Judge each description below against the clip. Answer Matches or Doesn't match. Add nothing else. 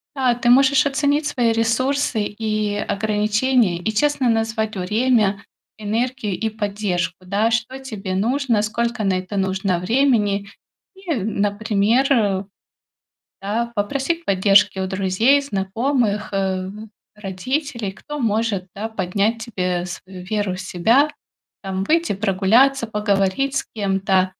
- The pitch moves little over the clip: Doesn't match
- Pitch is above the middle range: Matches